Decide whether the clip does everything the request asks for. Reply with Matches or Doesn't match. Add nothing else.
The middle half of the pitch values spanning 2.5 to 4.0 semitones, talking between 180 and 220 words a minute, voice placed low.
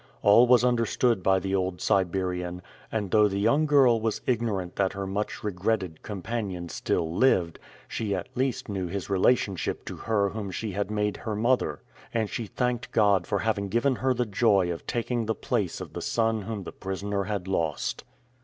Matches